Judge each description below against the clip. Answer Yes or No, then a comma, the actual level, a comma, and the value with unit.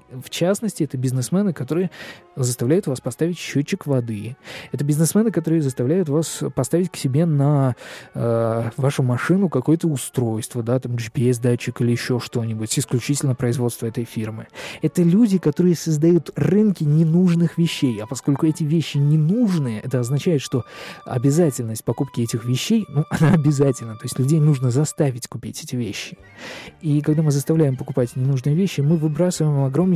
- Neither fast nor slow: Yes, average, 150 wpm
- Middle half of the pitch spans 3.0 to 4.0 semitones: No, average, 4.6 semitones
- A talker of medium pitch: Yes, medium, 145 Hz